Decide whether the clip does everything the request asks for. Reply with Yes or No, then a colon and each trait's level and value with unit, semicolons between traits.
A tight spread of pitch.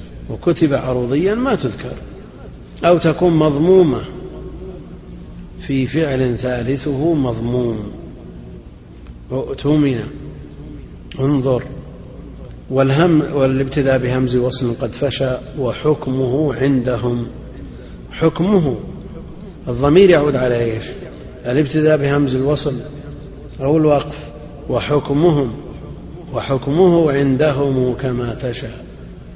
No: average, 3.2 semitones